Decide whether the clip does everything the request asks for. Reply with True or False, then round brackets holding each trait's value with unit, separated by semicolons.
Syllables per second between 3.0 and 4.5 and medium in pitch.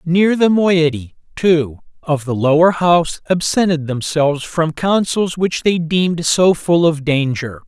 True (4.1 syllables/s; 165 Hz)